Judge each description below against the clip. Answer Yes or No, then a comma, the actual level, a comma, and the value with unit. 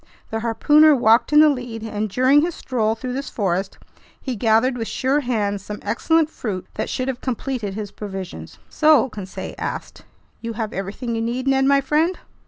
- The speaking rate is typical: Yes, average, 185 wpm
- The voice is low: No, high, 235 Hz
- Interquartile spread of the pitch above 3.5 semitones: Yes, average, 4.2 semitones